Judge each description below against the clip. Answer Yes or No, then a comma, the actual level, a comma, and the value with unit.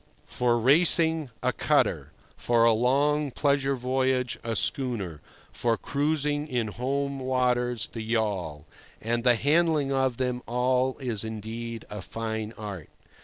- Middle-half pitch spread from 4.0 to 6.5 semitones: No, average, 3.3 semitones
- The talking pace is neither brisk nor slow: No, slow, 130 wpm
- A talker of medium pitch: No, low, 125 Hz